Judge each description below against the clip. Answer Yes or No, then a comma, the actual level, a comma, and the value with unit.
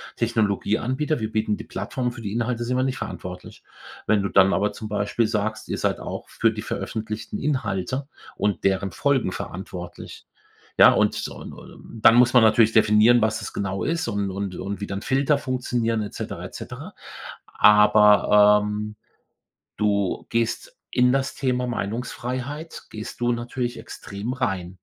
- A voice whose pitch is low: Yes, low, 110 Hz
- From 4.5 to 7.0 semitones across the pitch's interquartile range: No, average, 3.3 semitones